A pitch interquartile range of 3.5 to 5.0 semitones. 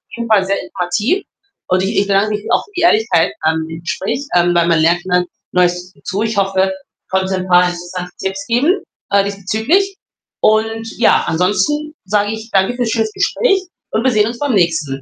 Yes: average, 4.1 semitones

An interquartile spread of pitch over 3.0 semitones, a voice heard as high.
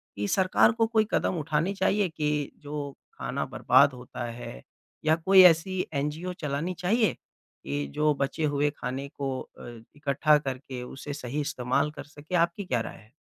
No: average, 4.6 semitones; medium, 150 Hz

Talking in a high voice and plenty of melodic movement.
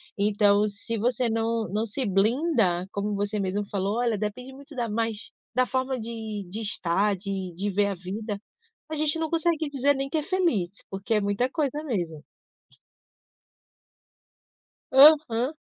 No: high, 225 Hz; average, 4.7 semitones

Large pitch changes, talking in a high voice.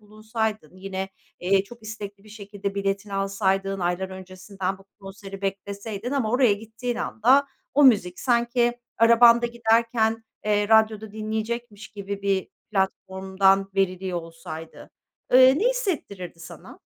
No: average, 2.9 semitones; high, 205 Hz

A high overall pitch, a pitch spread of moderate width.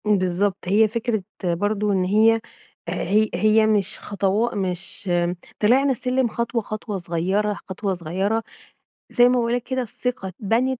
Yes: high, 210 Hz; average, 3.4 semitones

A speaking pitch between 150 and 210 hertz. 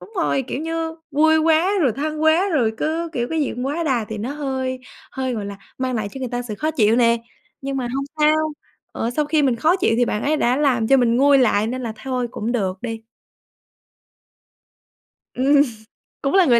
No: very high, 265 Hz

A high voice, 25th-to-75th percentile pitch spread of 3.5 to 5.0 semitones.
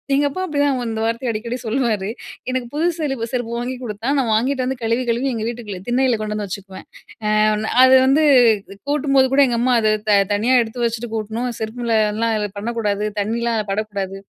No: high, 235 Hz; average, 3.1 semitones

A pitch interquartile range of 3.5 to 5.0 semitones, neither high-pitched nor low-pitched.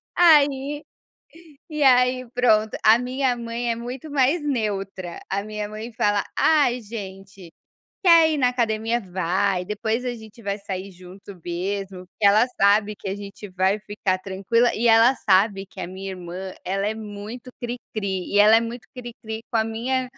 No: average, 3.8 semitones; high, 215 Hz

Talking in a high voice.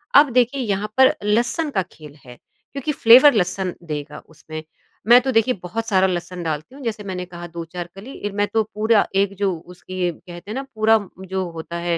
Yes: high, 200 Hz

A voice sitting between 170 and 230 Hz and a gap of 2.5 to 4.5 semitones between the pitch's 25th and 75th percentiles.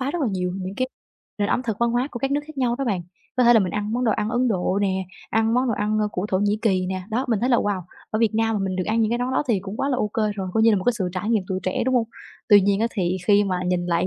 Yes: high, 215 Hz; average, 3.9 semitones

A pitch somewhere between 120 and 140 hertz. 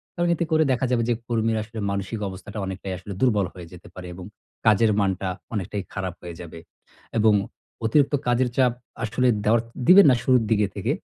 No: low, 110 Hz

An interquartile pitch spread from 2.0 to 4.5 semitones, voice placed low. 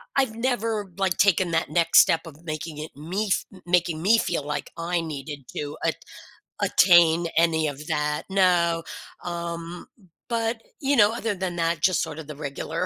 No: average, 3.3 semitones; medium, 170 Hz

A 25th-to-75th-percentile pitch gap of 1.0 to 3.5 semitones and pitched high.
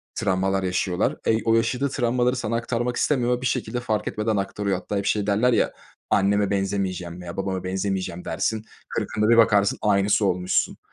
No: average, 3.2 semitones; low, 105 Hz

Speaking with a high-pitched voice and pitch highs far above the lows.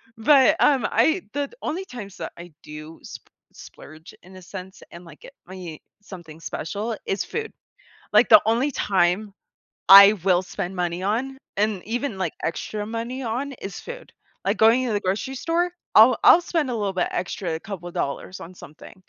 Yes: high, 205 Hz; wide, 6.2 semitones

